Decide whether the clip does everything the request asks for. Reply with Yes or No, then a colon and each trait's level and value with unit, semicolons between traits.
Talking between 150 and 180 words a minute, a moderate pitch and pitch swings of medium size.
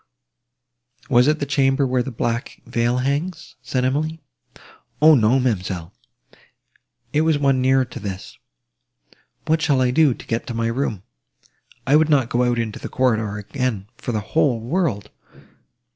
No: average, 160 wpm; low, 125 Hz; average, 3.6 semitones